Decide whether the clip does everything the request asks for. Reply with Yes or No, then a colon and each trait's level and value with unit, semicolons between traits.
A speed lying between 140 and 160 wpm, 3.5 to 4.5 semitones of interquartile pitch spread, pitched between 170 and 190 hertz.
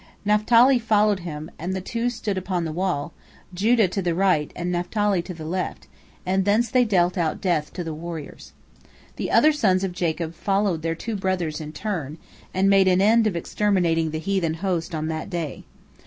No: average, 190 wpm; average, 3.8 semitones; medium, 185 Hz